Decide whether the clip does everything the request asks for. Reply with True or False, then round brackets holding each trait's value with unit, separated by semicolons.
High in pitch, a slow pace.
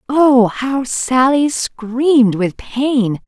True (255 Hz; 110 wpm)